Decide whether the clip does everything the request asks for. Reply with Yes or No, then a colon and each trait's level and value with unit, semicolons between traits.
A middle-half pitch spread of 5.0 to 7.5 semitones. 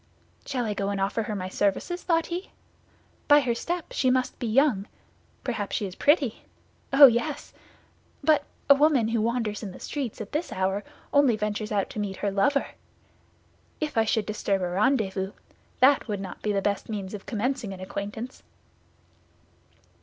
Yes: wide, 5.4 semitones